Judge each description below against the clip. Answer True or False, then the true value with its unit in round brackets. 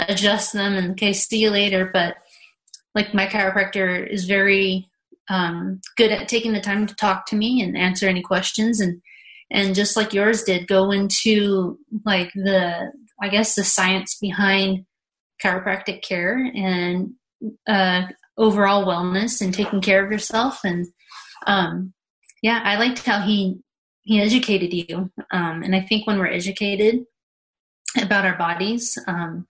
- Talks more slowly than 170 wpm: True (150 wpm)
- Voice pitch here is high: True (200 Hz)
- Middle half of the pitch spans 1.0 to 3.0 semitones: True (2.4 semitones)